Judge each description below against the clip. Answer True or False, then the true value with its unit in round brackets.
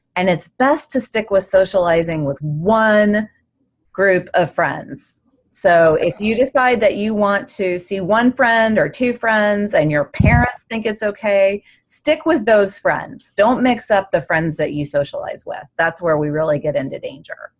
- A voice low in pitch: False (205 Hz)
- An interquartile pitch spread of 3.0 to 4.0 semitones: False (5.4 semitones)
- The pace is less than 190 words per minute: True (175 wpm)